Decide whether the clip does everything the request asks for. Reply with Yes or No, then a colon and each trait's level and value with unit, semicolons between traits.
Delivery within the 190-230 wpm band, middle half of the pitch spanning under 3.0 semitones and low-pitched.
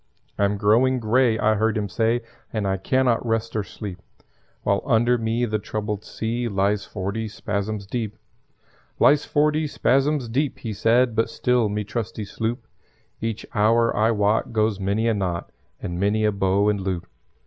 No: average, 170 wpm; narrow, 2.4 semitones; low, 110 Hz